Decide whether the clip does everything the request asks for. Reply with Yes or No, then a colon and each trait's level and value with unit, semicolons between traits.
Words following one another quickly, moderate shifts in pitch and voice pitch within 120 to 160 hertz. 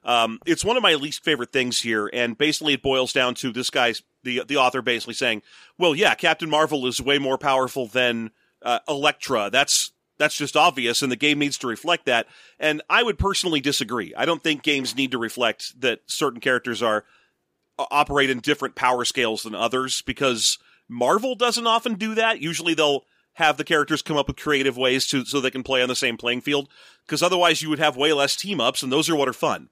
Yes: fast, 220 wpm; average, 3.2 semitones; medium, 140 Hz